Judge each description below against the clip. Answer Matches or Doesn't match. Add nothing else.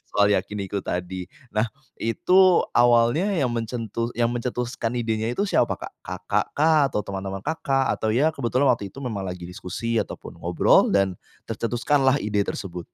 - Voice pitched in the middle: Doesn't match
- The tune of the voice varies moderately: Matches